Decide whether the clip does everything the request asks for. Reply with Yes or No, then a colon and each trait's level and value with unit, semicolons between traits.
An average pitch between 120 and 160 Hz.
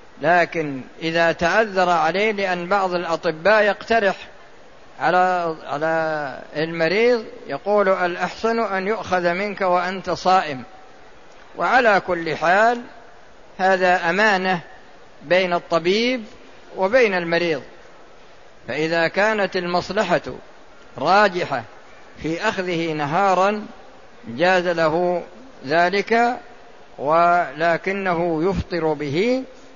No: medium, 180 Hz